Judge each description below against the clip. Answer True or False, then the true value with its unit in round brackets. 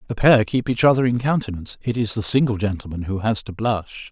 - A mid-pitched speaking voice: False (110 Hz)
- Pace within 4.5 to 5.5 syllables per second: False (5.9 syllables/s)